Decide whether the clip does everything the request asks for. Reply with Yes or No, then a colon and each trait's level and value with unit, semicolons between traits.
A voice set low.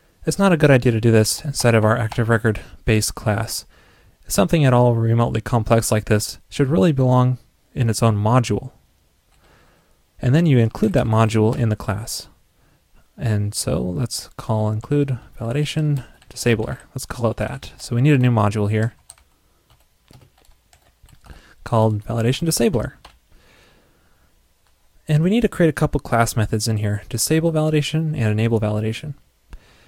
Yes: low, 115 Hz